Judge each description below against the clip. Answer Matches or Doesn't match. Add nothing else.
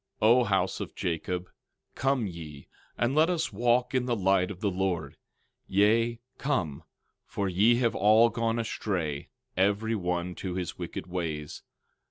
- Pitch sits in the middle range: Doesn't match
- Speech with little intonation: Doesn't match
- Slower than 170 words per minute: Matches